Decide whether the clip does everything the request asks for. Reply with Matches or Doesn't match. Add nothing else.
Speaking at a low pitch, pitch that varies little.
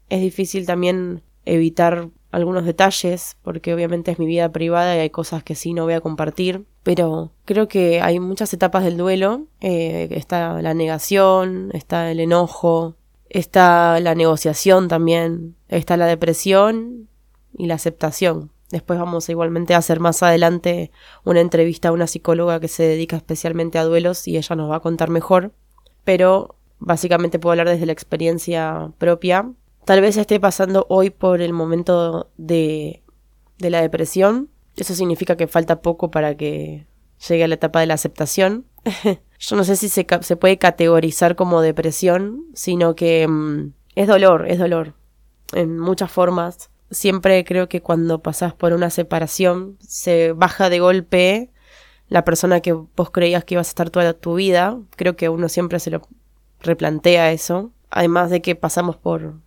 Doesn't match